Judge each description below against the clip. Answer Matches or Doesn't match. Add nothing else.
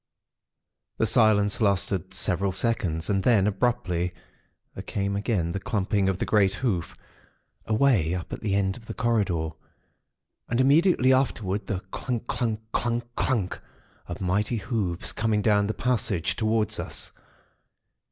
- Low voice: Matches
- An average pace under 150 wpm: Matches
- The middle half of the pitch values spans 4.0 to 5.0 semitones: Doesn't match